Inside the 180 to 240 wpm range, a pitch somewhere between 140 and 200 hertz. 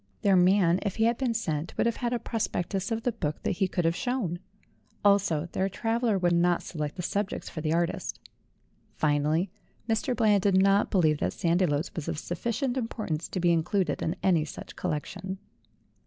Yes: average, 185 wpm; medium, 185 Hz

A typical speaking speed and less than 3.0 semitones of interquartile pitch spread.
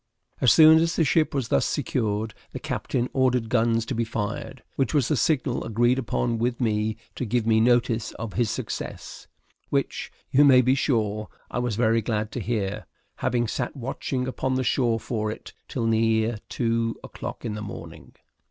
Yes: average, 180 wpm; narrow, 2.5 semitones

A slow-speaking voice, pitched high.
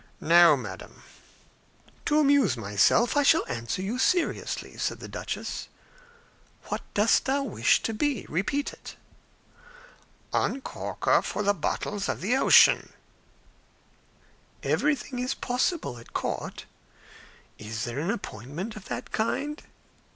Yes: slow, 120 wpm; high, 210 Hz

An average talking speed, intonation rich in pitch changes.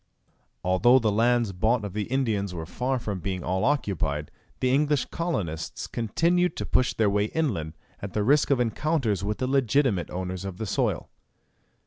Yes: average, 170 wpm; wide, 5.8 semitones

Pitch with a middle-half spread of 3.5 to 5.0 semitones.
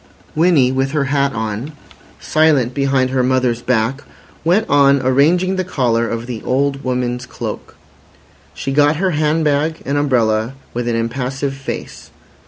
No: average, 2.9 semitones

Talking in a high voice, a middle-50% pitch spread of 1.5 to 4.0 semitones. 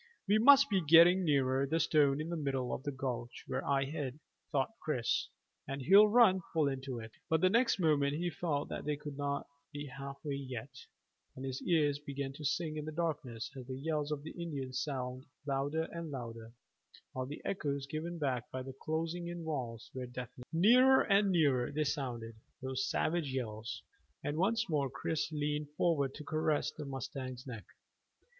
No: medium, 145 Hz; average, 3.6 semitones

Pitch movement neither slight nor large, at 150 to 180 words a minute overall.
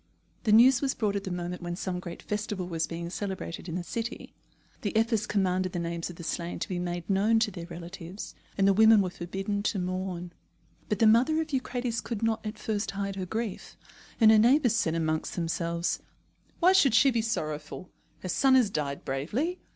No: average, 4.4 semitones; fast, 205 wpm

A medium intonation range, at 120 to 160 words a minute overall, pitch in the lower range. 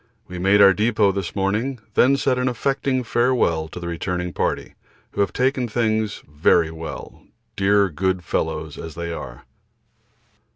No: wide, 5.9 semitones; average, 155 wpm; low, 100 Hz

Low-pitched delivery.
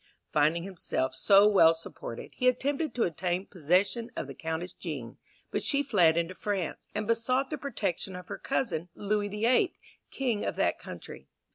No: high, 195 Hz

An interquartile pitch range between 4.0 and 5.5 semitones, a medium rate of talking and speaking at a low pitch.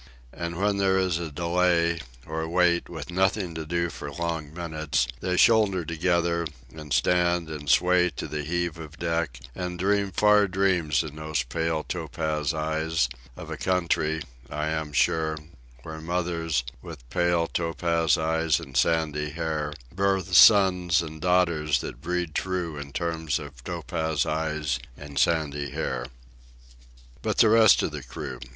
No: narrow, 2.4 semitones; average, 150 wpm; very low, 80 Hz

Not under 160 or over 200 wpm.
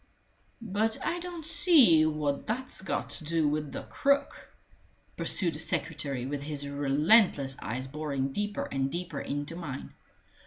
No: average, 145 wpm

